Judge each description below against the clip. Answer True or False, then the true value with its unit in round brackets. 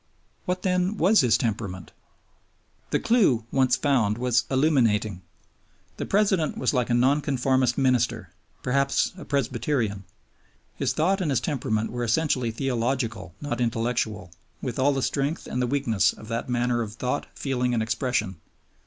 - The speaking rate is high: False (145 wpm)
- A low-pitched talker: True (125 Hz)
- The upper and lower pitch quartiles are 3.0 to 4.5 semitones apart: True (3.5 semitones)